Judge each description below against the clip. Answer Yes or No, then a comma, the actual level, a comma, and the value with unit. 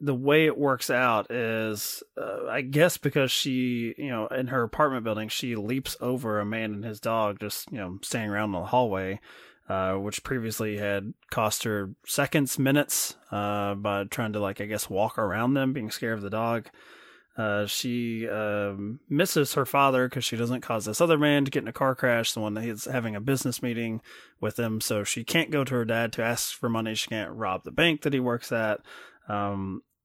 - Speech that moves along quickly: Yes, fast, 210 wpm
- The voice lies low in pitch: Yes, low, 115 Hz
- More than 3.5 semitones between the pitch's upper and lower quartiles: Yes, average, 3.9 semitones